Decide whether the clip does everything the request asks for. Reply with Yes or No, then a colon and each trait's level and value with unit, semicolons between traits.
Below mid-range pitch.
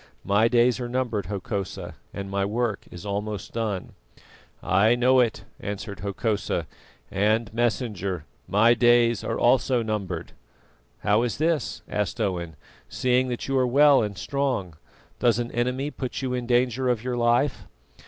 Yes: low, 115 Hz